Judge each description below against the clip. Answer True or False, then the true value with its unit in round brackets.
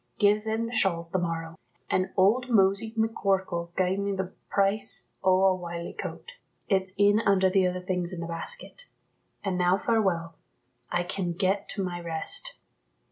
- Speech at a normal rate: True (165 wpm)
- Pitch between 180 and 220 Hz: True (190 Hz)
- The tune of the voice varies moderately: False (2.3 semitones)